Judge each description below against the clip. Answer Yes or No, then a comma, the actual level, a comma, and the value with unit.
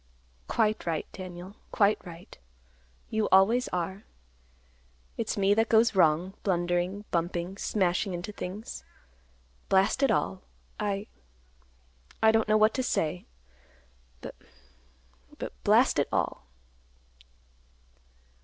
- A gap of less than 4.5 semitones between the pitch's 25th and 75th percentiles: No, average, 5.3 semitones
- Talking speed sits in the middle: No, slow, 100 wpm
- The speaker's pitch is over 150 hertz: Yes, medium, 185 Hz